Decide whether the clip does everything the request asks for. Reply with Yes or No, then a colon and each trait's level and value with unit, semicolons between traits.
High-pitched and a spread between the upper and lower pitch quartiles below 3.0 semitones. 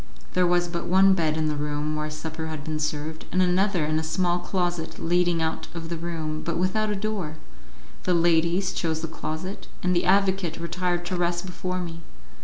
No: medium, 170 Hz; narrow, 2.4 semitones